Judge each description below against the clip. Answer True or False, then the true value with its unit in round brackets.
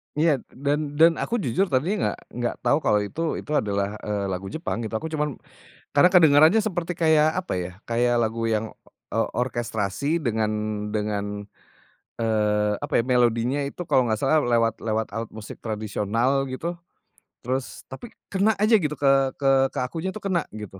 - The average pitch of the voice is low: True (125 Hz)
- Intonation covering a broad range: True (6.4 semitones)